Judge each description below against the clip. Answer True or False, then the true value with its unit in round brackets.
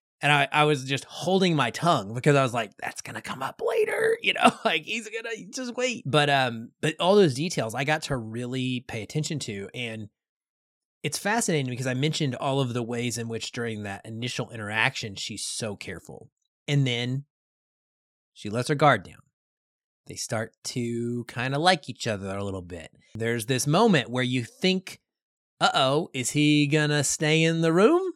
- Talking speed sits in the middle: True (190 wpm)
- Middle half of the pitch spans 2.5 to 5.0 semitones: False (5.4 semitones)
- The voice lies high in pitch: False (140 Hz)